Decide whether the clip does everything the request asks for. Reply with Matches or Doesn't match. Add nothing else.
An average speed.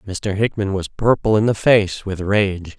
Matches